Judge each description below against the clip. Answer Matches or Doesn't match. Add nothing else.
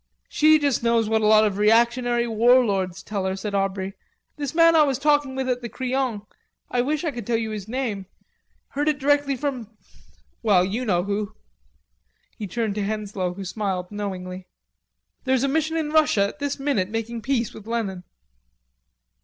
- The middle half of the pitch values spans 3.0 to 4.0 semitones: Doesn't match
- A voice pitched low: Doesn't match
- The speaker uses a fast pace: Doesn't match